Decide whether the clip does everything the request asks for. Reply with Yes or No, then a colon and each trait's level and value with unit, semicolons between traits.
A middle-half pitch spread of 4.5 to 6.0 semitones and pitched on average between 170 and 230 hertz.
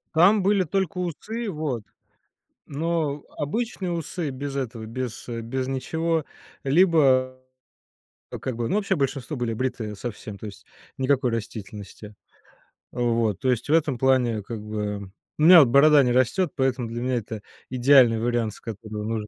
No: average, 5.1 semitones; low, 130 Hz